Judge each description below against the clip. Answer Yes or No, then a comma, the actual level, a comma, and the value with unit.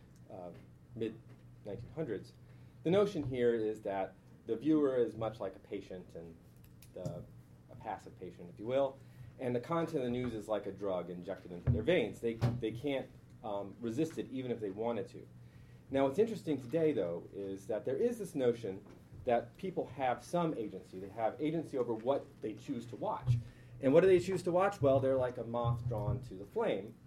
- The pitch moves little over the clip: No, average, 4.6 semitones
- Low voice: Yes, low, 120 Hz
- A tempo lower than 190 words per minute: No, average, 195 wpm